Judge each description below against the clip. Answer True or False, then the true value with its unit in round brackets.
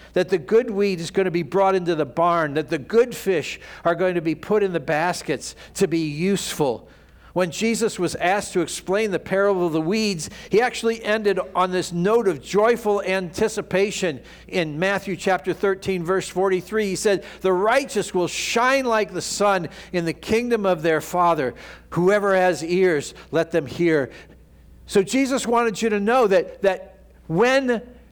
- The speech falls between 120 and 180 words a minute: True (175 wpm)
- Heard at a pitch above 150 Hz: True (190 Hz)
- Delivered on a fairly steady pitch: False (3.3 semitones)